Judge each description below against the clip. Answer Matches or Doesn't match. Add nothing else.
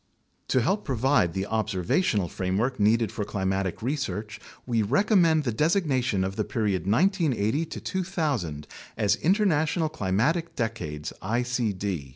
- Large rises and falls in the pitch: Matches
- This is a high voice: Doesn't match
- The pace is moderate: Doesn't match